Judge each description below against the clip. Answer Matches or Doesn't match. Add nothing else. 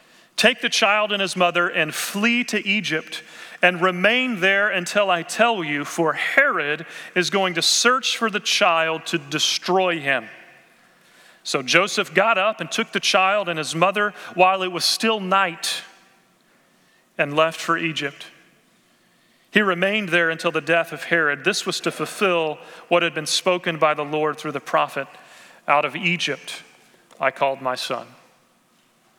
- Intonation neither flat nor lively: Matches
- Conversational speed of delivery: Matches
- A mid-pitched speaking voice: Matches